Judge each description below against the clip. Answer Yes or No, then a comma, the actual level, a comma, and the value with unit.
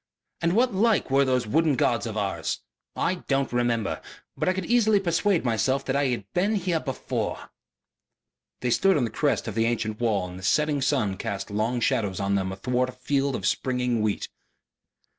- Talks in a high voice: No, low, 125 Hz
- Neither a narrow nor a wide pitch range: No, wide, 6.4 semitones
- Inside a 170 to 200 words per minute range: Yes, average, 190 wpm